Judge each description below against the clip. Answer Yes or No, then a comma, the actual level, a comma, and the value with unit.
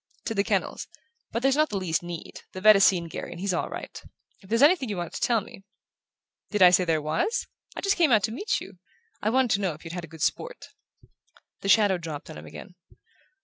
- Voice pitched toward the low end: No, high, 195 Hz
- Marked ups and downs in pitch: No, average, 5.0 semitones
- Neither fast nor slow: No, fast, 240 wpm